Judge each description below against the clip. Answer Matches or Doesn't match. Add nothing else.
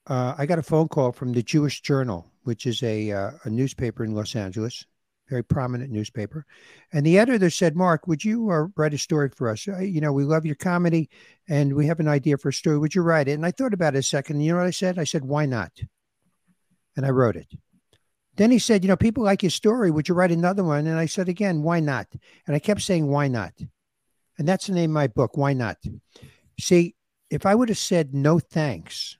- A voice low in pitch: Doesn't match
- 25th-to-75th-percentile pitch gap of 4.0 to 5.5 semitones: Matches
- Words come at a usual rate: Doesn't match